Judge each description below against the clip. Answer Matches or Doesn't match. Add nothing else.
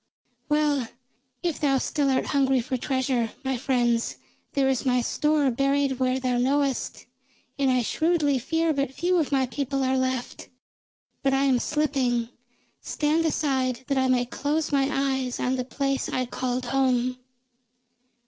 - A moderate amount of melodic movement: Doesn't match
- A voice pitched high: Matches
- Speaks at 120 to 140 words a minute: Doesn't match